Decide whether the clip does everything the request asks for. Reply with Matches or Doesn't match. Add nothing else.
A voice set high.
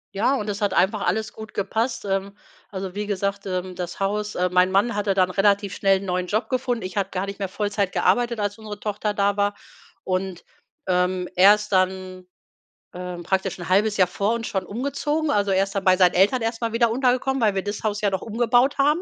Matches